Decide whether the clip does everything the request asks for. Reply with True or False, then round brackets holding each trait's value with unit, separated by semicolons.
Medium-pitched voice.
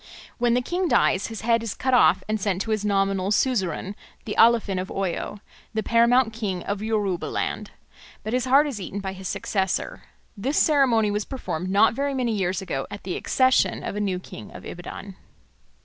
False (210 Hz)